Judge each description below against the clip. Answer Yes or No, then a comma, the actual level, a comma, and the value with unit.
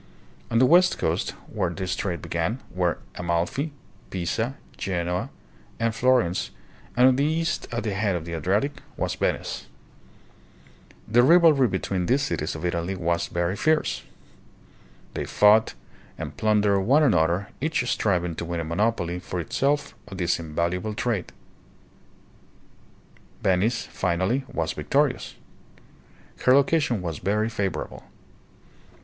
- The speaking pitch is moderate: No, low, 100 Hz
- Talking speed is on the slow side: Yes, slow, 130 wpm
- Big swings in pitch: Yes, wide, 6.3 semitones